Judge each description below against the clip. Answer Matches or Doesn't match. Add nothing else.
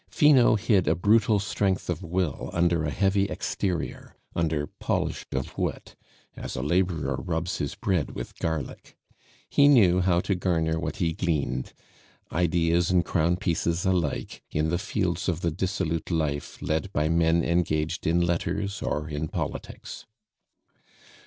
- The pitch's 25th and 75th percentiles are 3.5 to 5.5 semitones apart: Doesn't match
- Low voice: Matches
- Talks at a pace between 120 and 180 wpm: Matches